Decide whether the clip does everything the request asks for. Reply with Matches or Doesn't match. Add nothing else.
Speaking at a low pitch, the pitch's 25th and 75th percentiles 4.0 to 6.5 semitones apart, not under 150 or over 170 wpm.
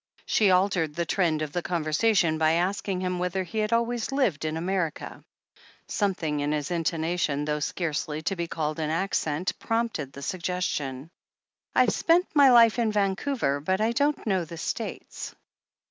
Doesn't match